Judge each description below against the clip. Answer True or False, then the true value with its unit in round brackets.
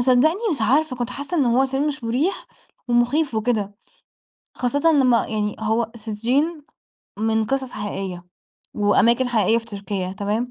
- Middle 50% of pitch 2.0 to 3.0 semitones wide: False (3.8 semitones)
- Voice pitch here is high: True (240 Hz)